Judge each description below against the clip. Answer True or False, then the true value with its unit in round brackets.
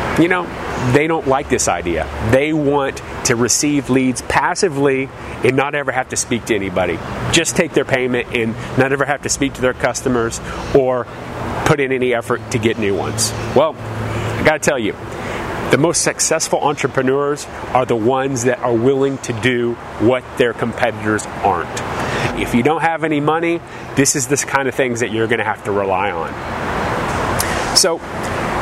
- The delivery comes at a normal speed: True (175 wpm)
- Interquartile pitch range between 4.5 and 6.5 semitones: False (3.0 semitones)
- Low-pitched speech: True (125 Hz)